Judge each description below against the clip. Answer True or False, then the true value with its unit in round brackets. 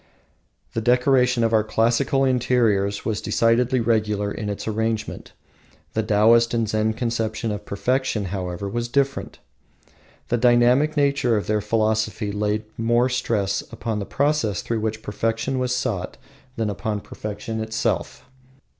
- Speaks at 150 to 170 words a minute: False (135 wpm)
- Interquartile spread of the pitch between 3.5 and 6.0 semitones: False (2.6 semitones)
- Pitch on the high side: False (115 Hz)